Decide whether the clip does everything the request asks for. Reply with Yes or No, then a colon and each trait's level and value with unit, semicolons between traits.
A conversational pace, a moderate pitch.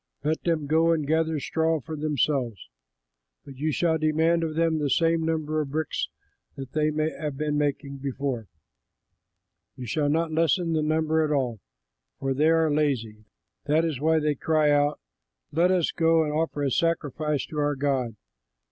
Yes: average, 170 wpm; medium, 155 Hz